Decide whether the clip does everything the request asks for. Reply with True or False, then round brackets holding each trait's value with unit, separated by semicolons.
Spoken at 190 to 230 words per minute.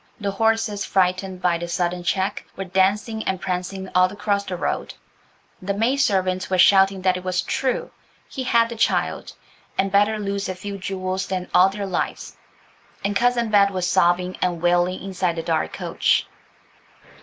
False (165 wpm)